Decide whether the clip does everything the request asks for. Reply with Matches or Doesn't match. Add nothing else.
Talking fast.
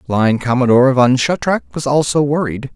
Doesn't match